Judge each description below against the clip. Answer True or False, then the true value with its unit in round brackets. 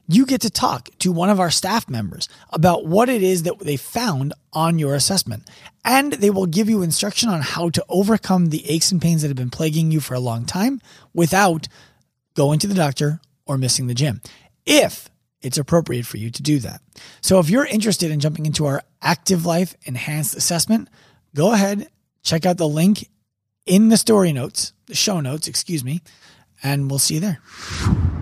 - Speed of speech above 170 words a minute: True (195 wpm)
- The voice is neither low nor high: True (165 Hz)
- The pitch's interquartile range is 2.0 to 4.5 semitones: False (5.3 semitones)